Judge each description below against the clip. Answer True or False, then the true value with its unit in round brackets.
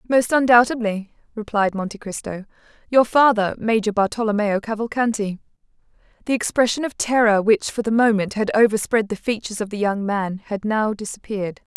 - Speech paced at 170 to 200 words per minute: False (150 wpm)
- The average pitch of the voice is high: True (215 Hz)